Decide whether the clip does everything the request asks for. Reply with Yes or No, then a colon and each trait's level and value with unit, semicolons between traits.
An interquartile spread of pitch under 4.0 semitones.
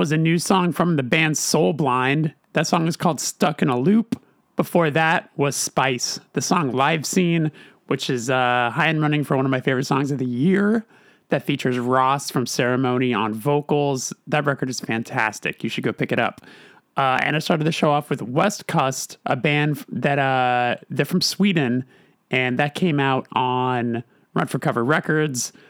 No: average, 4.3 semitones